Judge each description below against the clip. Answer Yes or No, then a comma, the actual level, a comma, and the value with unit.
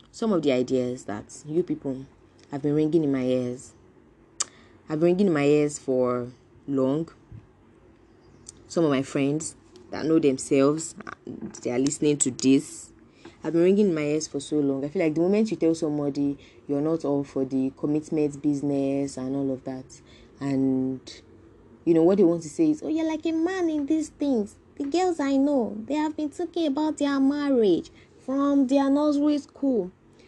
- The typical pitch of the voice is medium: Yes, medium, 150 Hz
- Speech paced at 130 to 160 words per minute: No, average, 185 wpm